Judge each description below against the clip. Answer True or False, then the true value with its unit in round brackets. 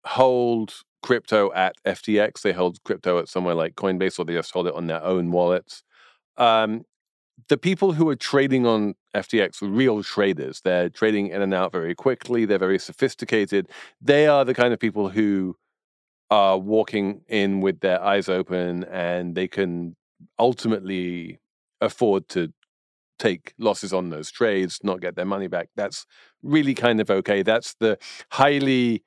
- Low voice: True (100 Hz)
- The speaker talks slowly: False (165 wpm)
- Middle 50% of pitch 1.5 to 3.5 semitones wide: False (4.5 semitones)